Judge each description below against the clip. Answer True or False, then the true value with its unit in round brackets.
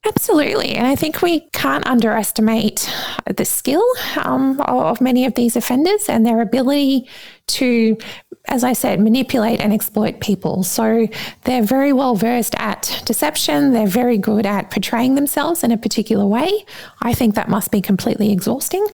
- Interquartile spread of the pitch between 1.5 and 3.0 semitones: False (3.7 semitones)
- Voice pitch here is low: False (240 Hz)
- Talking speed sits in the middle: True (160 wpm)